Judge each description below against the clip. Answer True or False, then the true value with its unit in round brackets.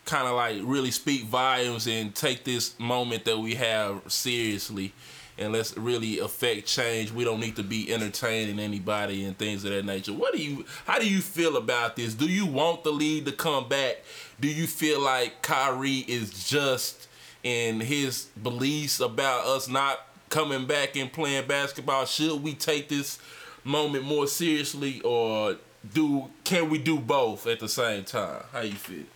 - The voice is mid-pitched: False (130 Hz)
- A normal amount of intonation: True (4.5 semitones)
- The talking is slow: False (175 wpm)